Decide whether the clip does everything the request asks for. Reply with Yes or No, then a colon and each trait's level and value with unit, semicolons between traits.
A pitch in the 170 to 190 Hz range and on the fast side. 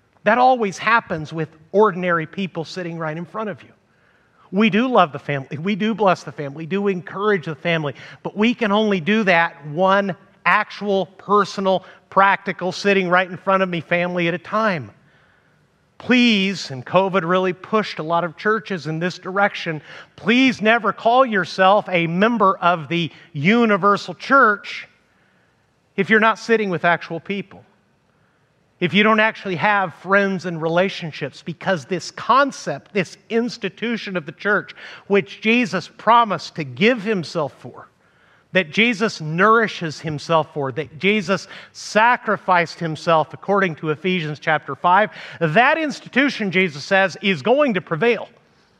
No: medium, 185 Hz; average, 150 wpm